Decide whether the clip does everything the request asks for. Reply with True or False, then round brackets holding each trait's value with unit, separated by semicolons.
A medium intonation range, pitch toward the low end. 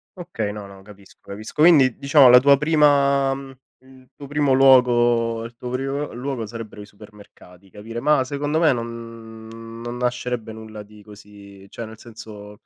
True (4.0 semitones; 120 Hz)